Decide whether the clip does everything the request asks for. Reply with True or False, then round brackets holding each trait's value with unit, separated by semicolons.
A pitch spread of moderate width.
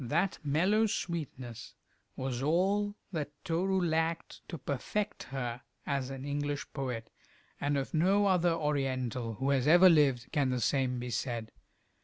True (4.9 semitones)